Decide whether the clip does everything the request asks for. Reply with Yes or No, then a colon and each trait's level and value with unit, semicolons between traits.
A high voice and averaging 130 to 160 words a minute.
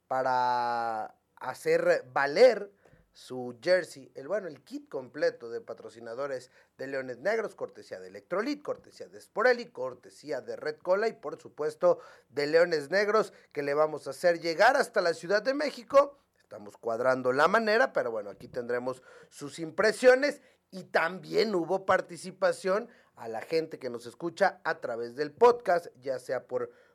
Yes: high, 205 Hz; average, 155 wpm